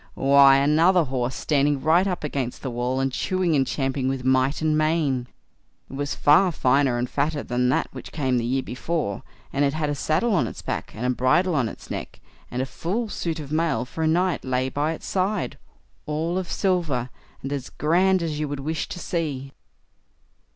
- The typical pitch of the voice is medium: Yes, medium, 145 Hz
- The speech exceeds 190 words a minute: Yes, average, 200 wpm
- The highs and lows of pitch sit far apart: No, average, 3.9 semitones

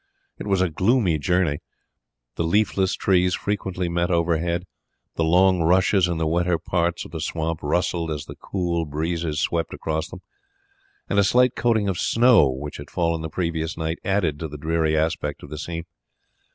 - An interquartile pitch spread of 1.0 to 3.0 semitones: Yes, narrow, 2.5 semitones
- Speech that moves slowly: No, average, 180 wpm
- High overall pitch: No, very low, 85 Hz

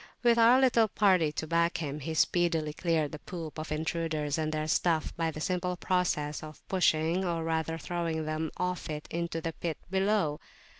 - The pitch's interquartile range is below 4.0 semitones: Yes, narrow, 2.5 semitones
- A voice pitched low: No, medium, 165 Hz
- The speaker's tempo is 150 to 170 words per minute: No, average, 185 wpm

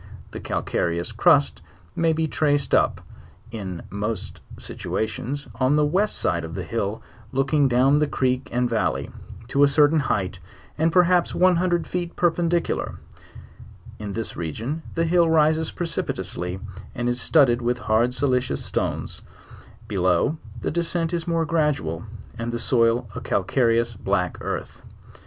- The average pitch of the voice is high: No, low, 130 Hz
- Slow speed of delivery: No, average, 145 wpm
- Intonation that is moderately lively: No, wide, 6.3 semitones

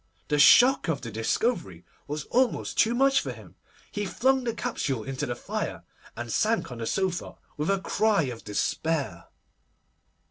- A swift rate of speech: No, average, 165 wpm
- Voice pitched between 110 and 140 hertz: No, medium, 165 Hz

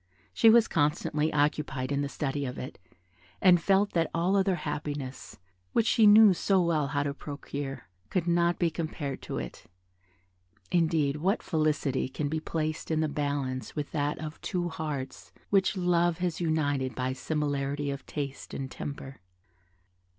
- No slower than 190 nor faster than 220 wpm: No, average, 160 wpm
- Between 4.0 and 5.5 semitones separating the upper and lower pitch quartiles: No, average, 3.4 semitones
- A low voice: No, medium, 150 Hz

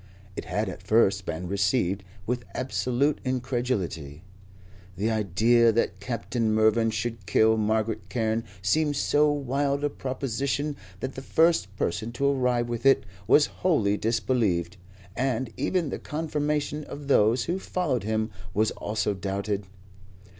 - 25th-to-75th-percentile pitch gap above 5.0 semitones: No, average, 4.5 semitones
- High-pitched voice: No, low, 115 Hz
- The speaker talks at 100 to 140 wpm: Yes, slow, 135 wpm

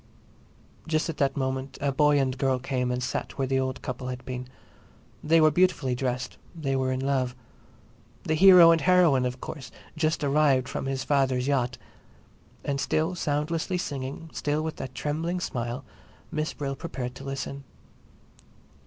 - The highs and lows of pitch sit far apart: No, average, 3.1 semitones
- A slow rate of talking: No, average, 165 wpm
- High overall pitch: No, low, 135 Hz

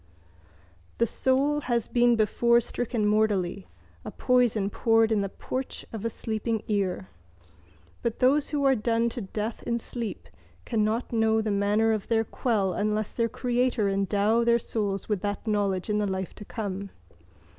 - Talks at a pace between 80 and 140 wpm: No, average, 160 wpm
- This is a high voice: Yes, high, 220 Hz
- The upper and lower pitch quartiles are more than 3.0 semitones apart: No, narrow, 2.5 semitones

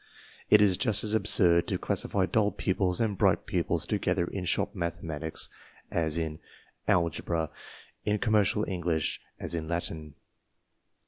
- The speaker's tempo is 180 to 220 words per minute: No, average, 140 wpm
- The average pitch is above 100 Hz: No, very low, 90 Hz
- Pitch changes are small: No, average, 3.8 semitones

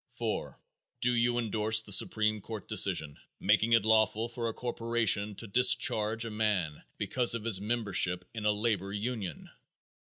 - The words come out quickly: No, average, 155 wpm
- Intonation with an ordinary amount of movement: No, narrow, 2.2 semitones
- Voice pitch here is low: Yes, low, 110 Hz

